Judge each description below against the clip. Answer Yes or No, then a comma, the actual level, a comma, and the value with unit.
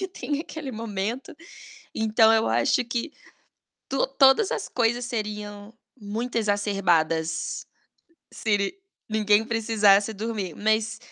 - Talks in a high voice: Yes, high, 220 Hz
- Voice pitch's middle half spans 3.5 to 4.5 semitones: No, average, 2.7 semitones